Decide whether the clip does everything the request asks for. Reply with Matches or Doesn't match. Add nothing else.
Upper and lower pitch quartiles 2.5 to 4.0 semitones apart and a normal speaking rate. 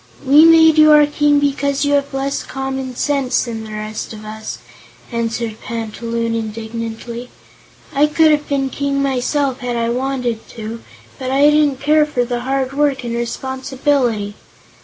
Matches